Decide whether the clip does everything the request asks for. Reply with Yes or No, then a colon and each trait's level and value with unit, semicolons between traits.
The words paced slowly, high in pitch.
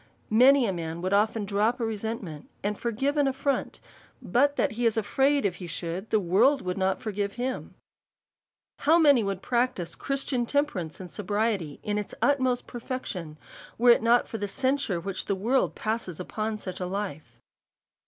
No: average, 175 wpm; high, 215 Hz